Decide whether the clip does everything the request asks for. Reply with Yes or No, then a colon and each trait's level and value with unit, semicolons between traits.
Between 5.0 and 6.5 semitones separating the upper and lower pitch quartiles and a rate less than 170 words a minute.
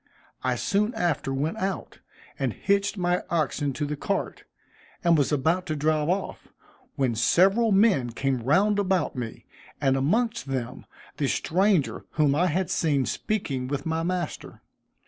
Yes: wide, 5.5 semitones; average, 150 wpm